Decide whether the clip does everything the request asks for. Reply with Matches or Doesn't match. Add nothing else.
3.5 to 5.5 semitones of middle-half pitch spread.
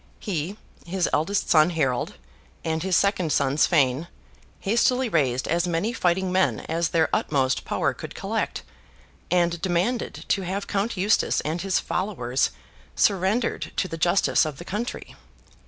Matches